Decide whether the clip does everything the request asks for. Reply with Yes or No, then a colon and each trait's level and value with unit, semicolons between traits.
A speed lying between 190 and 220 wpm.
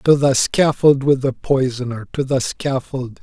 No: average, 150 wpm